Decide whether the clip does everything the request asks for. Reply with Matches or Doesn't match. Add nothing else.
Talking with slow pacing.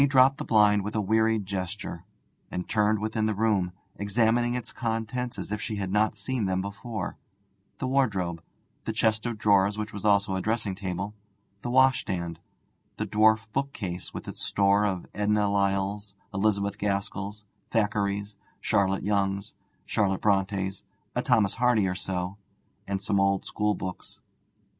Doesn't match